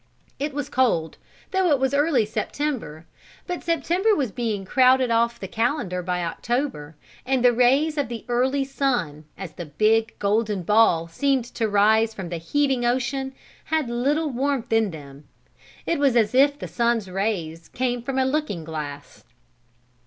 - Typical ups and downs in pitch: No, wide, 5.9 semitones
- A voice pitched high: Yes, high, 240 Hz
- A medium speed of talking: Yes, average, 160 wpm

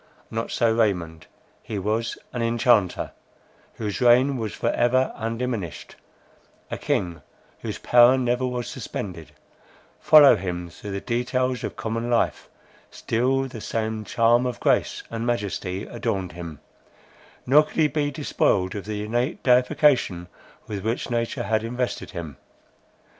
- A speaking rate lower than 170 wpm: Yes, slow, 135 wpm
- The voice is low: Yes, low, 115 Hz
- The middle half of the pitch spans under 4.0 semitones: Yes, average, 3.6 semitones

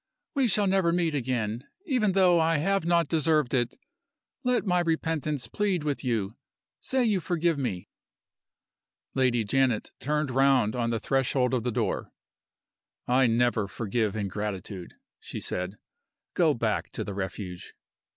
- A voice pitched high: No, low, 135 Hz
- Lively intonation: Yes, wide, 7.0 semitones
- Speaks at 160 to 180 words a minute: No, average, 140 wpm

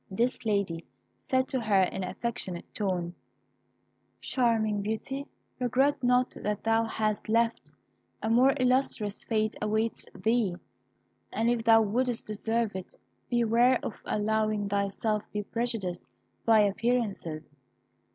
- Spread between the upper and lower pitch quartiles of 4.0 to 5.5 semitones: No, average, 2.7 semitones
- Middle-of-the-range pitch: No, high, 220 Hz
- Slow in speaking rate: Yes, slow, 125 wpm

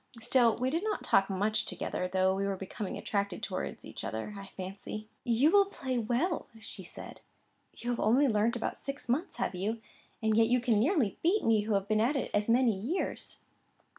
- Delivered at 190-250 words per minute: Yes, average, 200 wpm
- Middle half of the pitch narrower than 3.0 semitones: No, average, 4.4 semitones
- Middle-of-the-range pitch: No, high, 225 Hz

